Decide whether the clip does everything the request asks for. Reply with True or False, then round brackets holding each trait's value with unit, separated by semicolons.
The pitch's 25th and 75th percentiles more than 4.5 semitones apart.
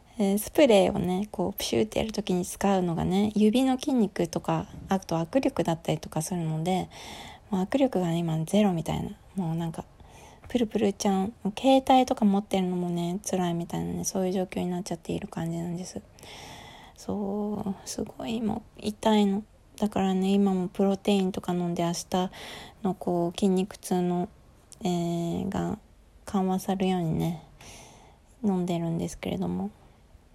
False (2.8 semitones)